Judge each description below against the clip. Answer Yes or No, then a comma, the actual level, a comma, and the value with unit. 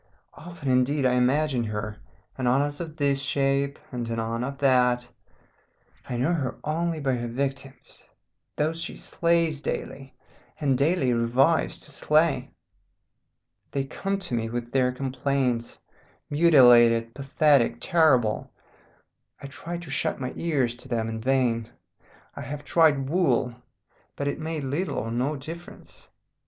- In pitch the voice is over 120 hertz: Yes, low, 135 Hz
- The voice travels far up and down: No, average, 3.8 semitones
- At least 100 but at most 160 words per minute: Yes, average, 140 wpm